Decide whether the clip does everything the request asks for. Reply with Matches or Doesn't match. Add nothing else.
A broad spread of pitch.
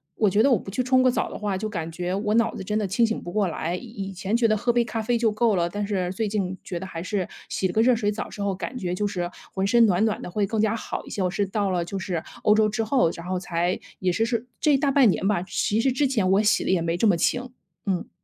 Doesn't match